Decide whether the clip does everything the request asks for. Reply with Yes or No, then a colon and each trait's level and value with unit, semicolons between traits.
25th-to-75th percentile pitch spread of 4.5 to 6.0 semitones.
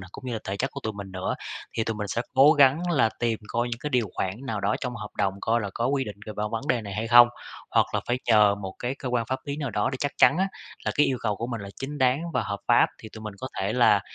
No: average, 3.9 semitones